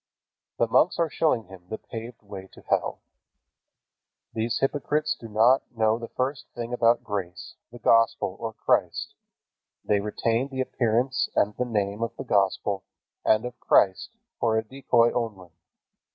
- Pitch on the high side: No, low, 115 Hz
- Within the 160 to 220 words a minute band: No, average, 150 wpm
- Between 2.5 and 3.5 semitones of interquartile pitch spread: Yes, average, 2.9 semitones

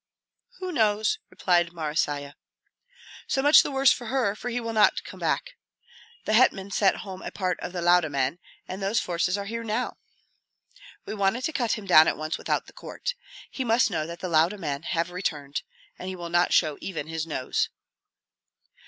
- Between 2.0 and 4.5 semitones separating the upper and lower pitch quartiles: No, average, 5.3 semitones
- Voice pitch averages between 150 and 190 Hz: Yes, medium, 185 Hz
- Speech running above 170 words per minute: Yes, average, 190 wpm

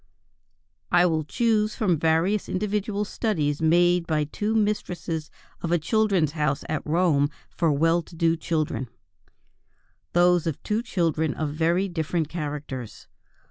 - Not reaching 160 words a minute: Yes, slow, 135 wpm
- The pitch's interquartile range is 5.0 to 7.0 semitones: No, average, 3.3 semitones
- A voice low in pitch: No, medium, 165 Hz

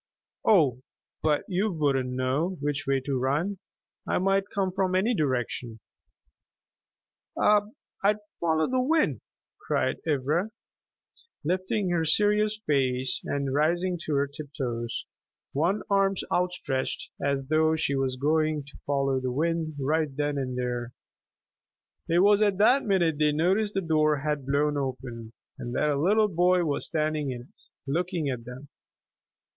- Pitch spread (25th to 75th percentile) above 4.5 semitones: Yes, average, 5.3 semitones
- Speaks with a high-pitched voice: No, medium, 155 Hz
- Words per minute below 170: Yes, average, 140 wpm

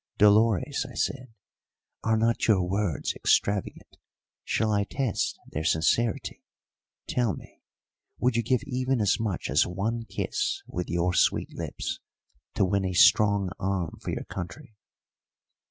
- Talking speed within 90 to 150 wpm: Yes, average, 140 wpm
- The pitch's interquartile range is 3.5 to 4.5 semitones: Yes, average, 4.0 semitones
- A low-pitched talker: Yes, low, 100 Hz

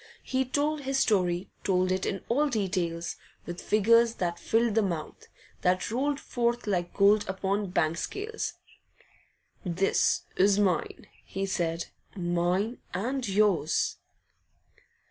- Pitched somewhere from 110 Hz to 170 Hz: No, high, 195 Hz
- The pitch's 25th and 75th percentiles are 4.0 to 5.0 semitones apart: Yes, average, 4.7 semitones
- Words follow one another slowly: Yes, slow, 130 wpm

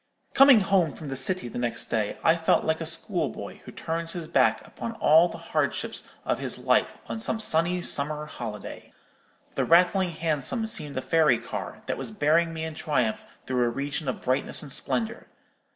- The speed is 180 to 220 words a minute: Yes, average, 185 wpm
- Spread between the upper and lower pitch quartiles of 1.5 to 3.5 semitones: No, average, 4.0 semitones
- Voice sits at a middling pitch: Yes, medium, 160 Hz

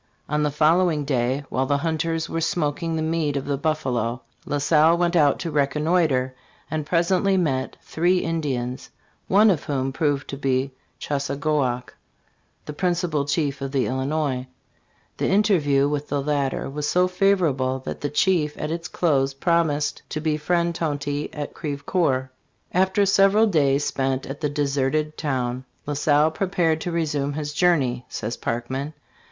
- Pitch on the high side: No, medium, 150 Hz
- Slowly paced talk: No, average, 160 wpm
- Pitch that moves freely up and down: No, average, 3.3 semitones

